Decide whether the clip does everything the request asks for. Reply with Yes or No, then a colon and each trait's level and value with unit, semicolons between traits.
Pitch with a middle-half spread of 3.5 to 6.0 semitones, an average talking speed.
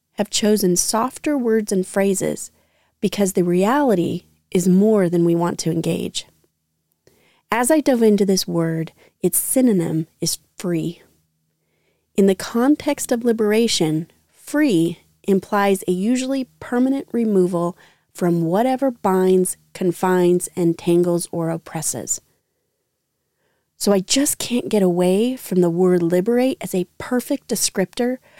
No: average, 5.1 semitones; slow, 125 wpm